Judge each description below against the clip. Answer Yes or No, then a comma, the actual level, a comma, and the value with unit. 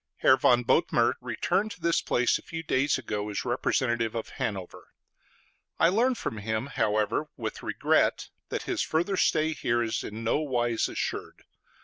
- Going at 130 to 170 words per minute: Yes, average, 160 wpm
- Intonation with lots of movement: Yes, wide, 5.9 semitones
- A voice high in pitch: No, low, 120 Hz